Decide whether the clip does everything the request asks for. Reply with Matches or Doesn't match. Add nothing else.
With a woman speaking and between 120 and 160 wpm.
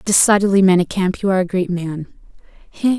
Matches